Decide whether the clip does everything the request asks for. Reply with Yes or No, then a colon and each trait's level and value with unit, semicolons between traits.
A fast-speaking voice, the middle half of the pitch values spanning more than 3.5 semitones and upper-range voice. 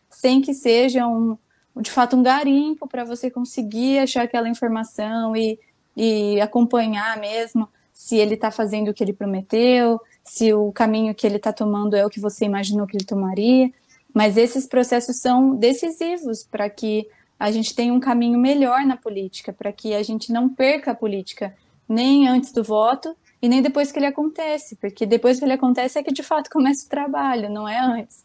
No: fast, 190 wpm; average, 3.2 semitones; high, 235 Hz